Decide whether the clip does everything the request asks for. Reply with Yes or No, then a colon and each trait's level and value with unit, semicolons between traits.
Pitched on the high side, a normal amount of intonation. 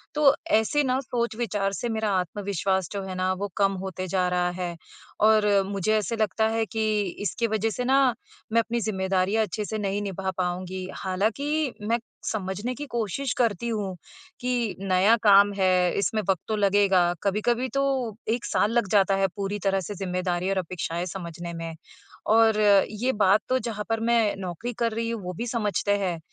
Yes: high, 205 Hz; average, 3.2 semitones